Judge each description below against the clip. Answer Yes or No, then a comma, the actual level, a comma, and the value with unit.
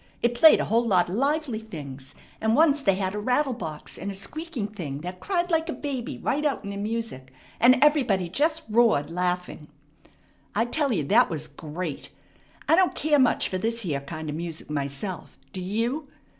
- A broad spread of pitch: Yes, wide, 7.9 semitones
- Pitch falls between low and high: No, high, 215 Hz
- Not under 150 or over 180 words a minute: No, average, 195 wpm